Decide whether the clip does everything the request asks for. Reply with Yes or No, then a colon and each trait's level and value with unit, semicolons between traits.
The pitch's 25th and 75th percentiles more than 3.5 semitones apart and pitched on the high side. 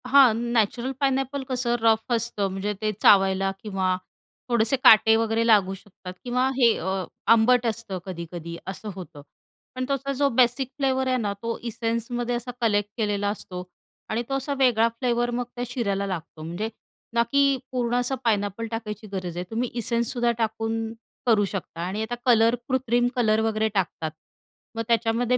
No: average, 3.2 semitones; high, 225 Hz